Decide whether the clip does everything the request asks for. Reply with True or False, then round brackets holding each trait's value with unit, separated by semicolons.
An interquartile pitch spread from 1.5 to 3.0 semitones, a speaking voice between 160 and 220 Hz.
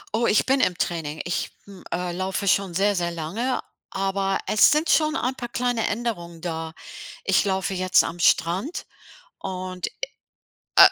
False (4.4 semitones; 190 Hz)